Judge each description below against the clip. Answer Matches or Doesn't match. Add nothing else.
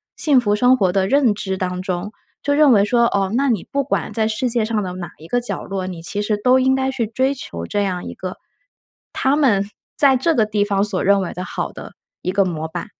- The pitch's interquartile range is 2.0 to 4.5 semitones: Doesn't match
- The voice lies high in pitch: Matches